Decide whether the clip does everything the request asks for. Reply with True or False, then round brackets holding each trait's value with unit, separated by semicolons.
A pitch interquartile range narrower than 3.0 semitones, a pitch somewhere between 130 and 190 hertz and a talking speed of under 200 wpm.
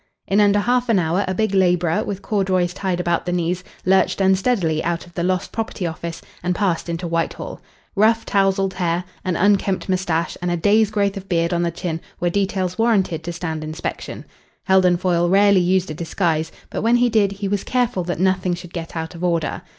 False (2.6 semitones; 185 Hz; 205 wpm)